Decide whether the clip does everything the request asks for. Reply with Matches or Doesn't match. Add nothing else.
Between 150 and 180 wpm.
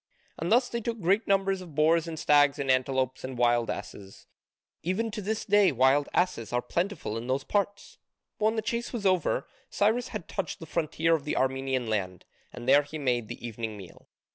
Doesn't match